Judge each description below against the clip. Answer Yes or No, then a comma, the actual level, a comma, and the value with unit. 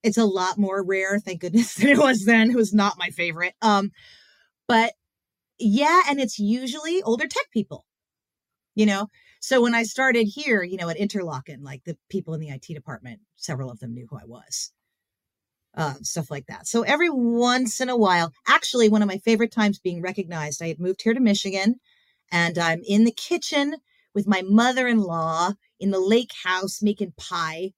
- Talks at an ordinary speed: Yes, average, 190 wpm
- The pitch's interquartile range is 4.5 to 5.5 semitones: Yes, average, 5.0 semitones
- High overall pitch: Yes, high, 205 Hz